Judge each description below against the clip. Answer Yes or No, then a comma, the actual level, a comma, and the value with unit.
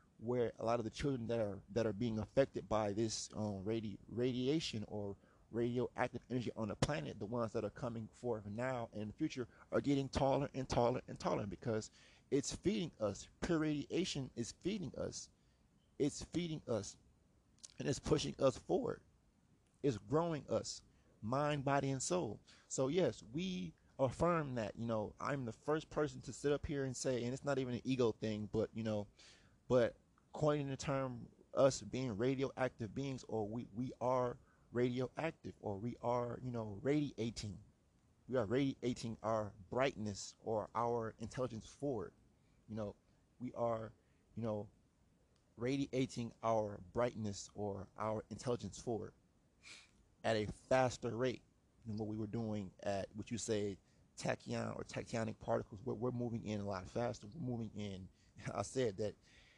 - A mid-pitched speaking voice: No, low, 115 Hz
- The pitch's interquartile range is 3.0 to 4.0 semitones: Yes, average, 3.4 semitones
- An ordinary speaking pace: Yes, average, 160 wpm